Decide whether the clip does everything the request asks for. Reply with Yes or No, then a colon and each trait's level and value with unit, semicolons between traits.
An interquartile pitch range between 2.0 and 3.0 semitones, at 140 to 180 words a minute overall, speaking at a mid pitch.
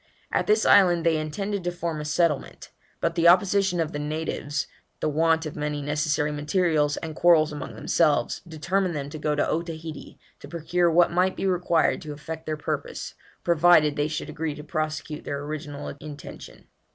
Yes: narrow, 2.5 semitones; average, 175 wpm; medium, 155 Hz